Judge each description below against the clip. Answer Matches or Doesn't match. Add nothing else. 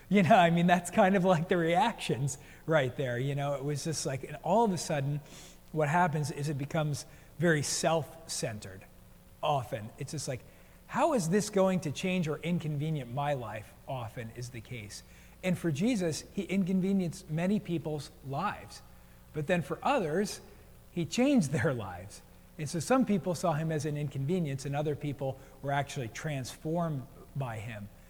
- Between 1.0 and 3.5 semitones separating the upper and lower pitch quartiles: Doesn't match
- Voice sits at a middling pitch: Matches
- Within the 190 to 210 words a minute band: Doesn't match